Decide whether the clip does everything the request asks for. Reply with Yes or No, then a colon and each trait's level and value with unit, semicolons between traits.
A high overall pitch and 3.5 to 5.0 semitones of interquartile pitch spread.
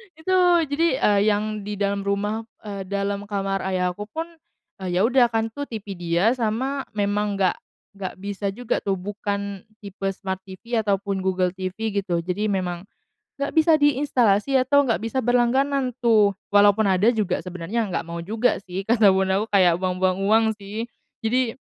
No: high, 205 Hz; average, 2.9 semitones